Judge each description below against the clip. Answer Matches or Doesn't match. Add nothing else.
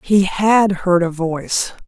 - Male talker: Doesn't match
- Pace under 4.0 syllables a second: Matches